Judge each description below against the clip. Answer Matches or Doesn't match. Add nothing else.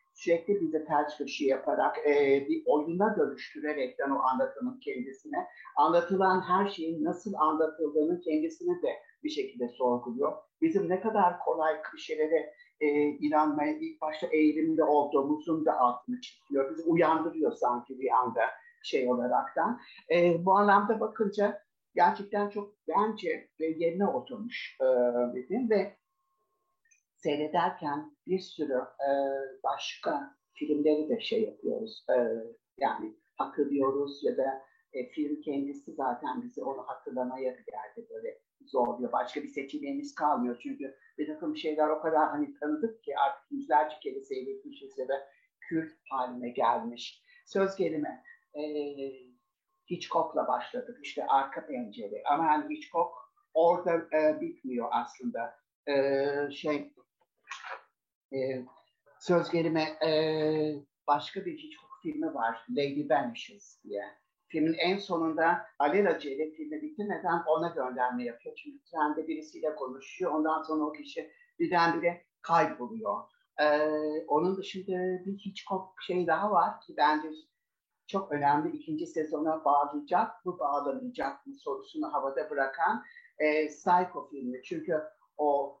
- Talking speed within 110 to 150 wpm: Matches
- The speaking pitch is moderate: Matches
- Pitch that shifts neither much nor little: Doesn't match